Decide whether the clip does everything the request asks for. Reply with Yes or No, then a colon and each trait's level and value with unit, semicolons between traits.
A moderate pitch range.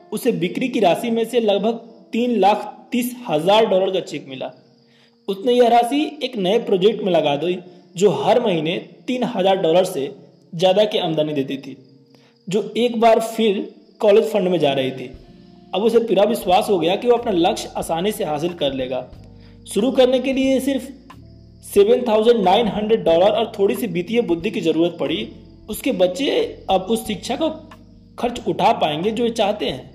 Yes: average, 4.9 semitones